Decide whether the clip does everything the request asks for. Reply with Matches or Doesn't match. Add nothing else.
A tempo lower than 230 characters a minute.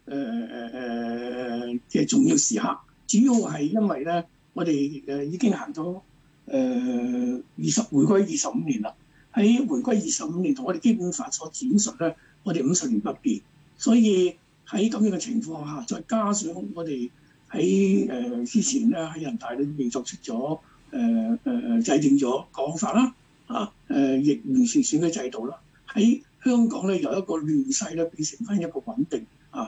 Doesn't match